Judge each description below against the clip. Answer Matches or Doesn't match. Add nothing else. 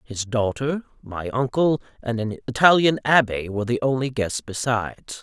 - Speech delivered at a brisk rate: Doesn't match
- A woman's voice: Doesn't match